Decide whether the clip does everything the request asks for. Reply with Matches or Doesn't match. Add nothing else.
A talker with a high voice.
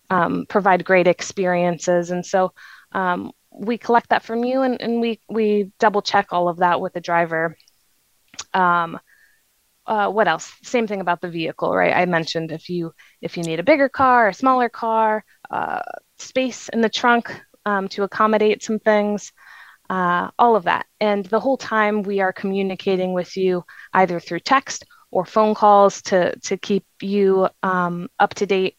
Matches